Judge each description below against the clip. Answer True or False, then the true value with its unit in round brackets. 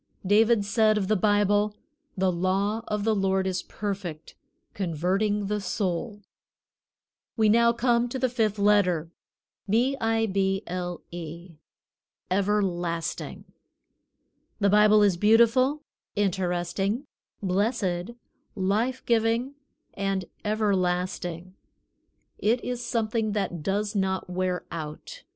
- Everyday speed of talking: False (110 wpm)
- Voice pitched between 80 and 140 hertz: False (205 Hz)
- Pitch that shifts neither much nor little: True (3.2 semitones)